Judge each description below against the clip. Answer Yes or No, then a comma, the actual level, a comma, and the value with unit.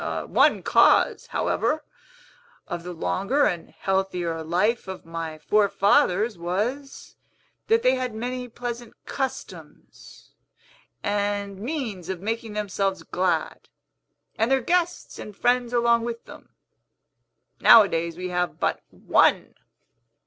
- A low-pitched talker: No, high, 205 Hz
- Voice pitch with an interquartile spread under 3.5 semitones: No, average, 5.1 semitones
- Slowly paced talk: Yes, slow, 115 wpm